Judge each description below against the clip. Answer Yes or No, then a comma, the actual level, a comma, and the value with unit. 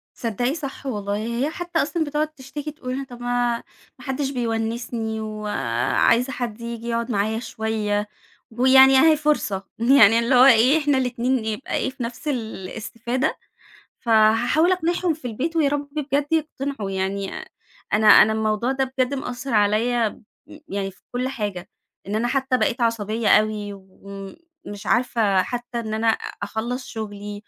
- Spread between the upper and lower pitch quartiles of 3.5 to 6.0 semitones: Yes, average, 3.8 semitones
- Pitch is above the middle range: Yes, high, 235 Hz